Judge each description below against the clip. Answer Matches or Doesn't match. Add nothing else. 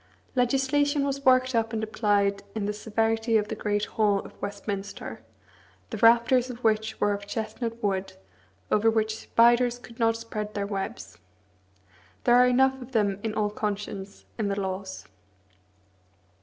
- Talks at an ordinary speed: Matches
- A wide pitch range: Doesn't match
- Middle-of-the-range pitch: Doesn't match